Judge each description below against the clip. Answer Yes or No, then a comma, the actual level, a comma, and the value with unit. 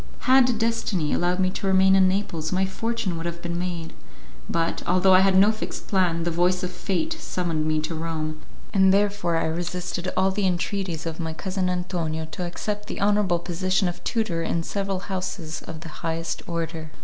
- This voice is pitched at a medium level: Yes, medium, 180 Hz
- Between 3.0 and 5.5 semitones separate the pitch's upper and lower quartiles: No, narrow, 2.6 semitones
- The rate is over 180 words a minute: Yes, average, 190 wpm